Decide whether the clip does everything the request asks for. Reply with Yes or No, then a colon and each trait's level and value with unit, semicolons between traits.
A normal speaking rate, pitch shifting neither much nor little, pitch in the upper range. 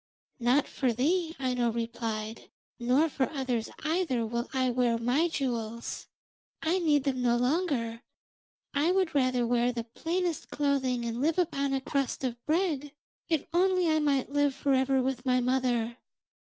Yes: average, 155 wpm; average, 3.8 semitones; very high, 265 Hz